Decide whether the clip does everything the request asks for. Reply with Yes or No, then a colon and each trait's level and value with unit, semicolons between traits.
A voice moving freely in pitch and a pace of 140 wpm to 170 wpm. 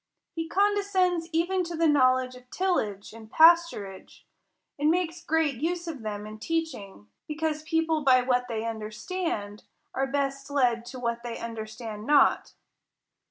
Yes: wide, 6.3 semitones; average, 150 wpm